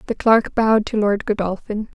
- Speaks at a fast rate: No, average, 180 wpm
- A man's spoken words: No, female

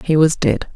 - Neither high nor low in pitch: Yes, medium, 155 Hz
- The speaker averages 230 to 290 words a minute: Yes, fast, 240 wpm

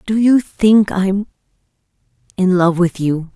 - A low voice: No, high, 190 Hz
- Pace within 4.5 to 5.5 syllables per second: No, 3.8 syllables/s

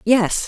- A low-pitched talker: No, high, 215 Hz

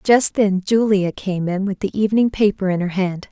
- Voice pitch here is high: Yes, high, 200 Hz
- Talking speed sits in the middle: No, fast, 215 wpm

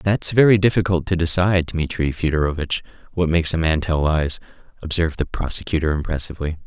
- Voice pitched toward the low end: Yes, very low, 85 Hz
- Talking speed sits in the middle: Yes, average, 155 wpm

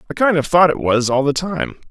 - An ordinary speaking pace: No, fast, 285 wpm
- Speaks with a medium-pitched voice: Yes, medium, 155 Hz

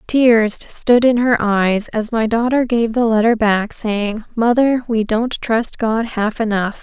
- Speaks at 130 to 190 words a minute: Yes, average, 175 wpm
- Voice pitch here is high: Yes, high, 225 Hz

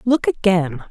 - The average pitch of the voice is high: Yes, high, 210 Hz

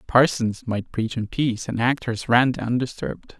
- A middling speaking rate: Yes, average, 160 wpm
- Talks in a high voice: No, low, 115 Hz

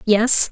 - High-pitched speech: Yes, high, 225 Hz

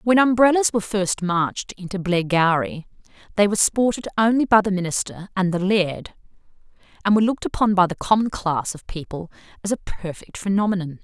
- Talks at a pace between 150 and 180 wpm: Yes, average, 170 wpm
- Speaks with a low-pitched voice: No, high, 195 Hz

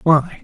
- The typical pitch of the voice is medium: Yes, medium, 155 Hz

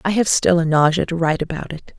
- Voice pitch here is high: No, medium, 170 Hz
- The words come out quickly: Yes, fast, 270 wpm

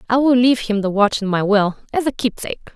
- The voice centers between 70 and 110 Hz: No, high, 225 Hz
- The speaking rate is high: Yes, fast, 260 wpm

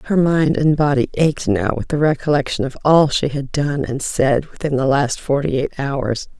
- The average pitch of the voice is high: No, medium, 140 Hz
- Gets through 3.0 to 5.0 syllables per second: Yes, 4.8 syllables/s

